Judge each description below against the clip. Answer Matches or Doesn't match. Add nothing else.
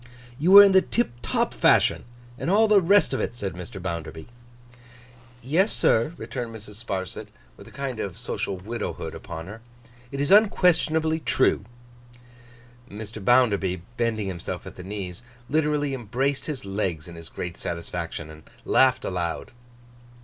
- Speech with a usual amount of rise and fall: Doesn't match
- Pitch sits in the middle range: Doesn't match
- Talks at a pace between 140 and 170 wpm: Matches